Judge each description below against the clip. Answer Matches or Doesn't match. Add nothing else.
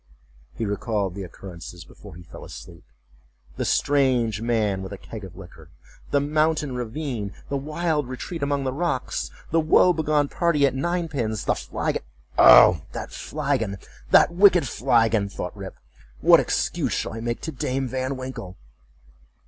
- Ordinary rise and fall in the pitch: Doesn't match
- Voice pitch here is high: Doesn't match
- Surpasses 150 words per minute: Doesn't match